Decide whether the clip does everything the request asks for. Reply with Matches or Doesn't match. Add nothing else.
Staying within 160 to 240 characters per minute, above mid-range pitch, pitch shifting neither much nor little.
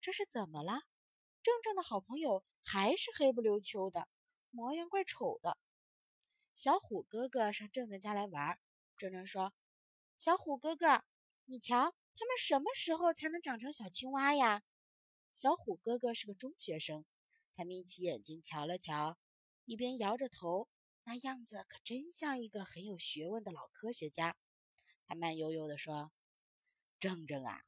Doesn't match